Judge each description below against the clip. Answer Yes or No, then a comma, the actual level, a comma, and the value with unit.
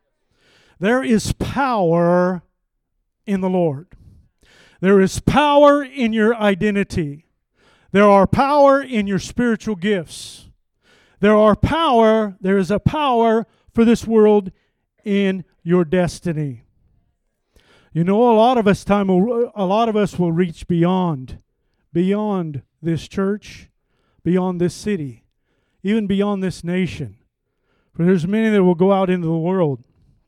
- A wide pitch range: No, average, 3.6 semitones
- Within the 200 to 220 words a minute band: No, slow, 135 wpm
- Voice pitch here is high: Yes, high, 195 Hz